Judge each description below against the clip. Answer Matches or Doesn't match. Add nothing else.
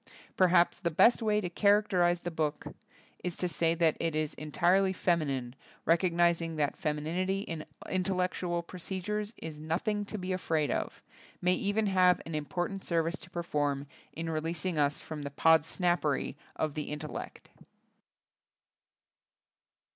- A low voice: Doesn't match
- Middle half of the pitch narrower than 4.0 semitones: Matches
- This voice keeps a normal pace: Matches